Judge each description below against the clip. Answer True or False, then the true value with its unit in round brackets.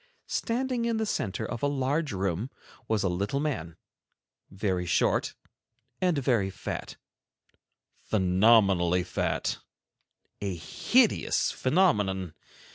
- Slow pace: True (105 wpm)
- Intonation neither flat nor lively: False (7.4 semitones)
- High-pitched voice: False (105 Hz)